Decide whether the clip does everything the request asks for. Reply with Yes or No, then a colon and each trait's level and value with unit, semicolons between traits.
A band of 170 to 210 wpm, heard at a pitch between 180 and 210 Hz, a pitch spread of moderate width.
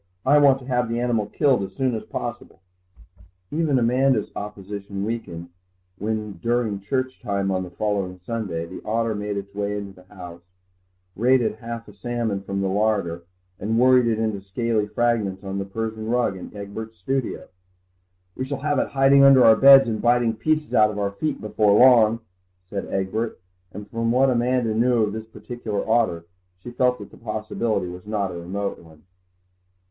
No: average, 180 wpm; low, 110 Hz; average, 3.4 semitones